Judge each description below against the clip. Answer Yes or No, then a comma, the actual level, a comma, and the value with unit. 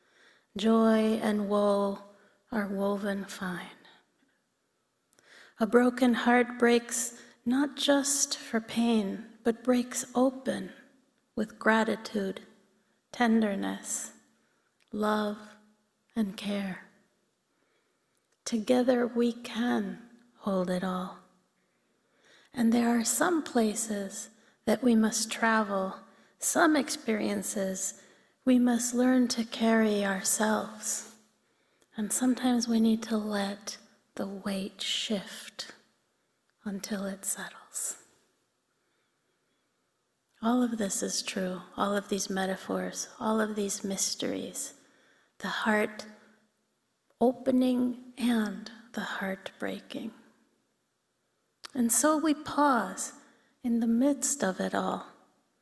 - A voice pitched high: Yes, high, 220 Hz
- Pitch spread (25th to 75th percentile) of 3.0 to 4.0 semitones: Yes, average, 3.4 semitones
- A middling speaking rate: No, slow, 95 wpm